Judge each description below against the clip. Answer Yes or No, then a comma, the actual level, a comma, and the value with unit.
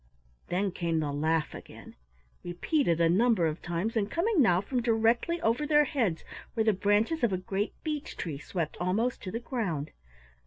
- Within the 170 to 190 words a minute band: Yes, average, 180 wpm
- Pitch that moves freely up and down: Yes, wide, 6.0 semitones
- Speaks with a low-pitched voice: No, high, 205 Hz